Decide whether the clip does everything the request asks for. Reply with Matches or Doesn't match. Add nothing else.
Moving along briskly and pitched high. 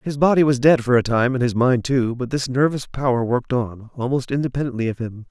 Doesn't match